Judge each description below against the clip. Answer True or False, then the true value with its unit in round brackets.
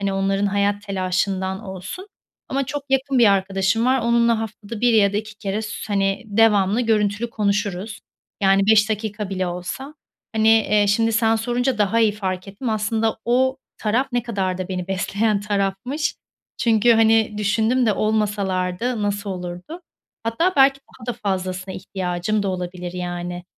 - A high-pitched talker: True (210 Hz)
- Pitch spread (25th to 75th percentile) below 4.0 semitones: True (2.8 semitones)